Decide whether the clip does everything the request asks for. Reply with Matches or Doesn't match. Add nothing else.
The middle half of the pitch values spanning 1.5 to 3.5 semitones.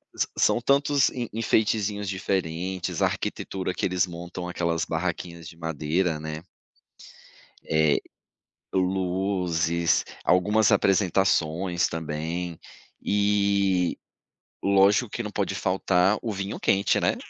Matches